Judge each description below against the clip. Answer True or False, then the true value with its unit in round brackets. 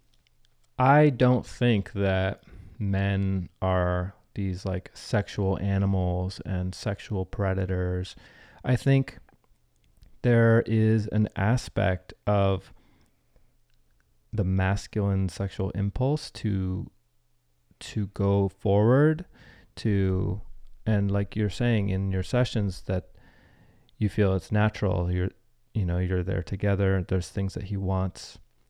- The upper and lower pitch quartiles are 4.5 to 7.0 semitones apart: False (2.4 semitones)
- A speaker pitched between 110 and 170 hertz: False (95 Hz)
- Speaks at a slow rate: True (110 wpm)